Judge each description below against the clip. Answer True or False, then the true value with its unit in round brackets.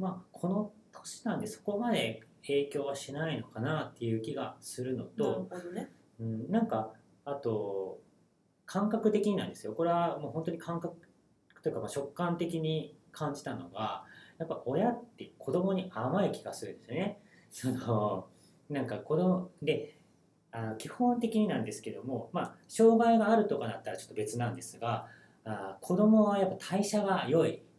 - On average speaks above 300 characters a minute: False (290 characters per minute)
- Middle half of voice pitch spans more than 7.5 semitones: True (8.0 semitones)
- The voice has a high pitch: False (165 Hz)